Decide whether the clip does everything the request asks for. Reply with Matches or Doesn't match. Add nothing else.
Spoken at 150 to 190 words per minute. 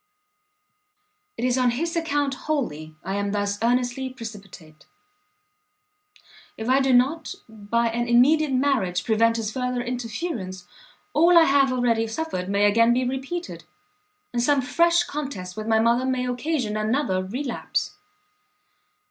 Doesn't match